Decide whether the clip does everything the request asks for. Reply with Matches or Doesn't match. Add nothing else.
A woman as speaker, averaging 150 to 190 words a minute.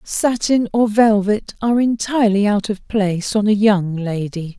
Matches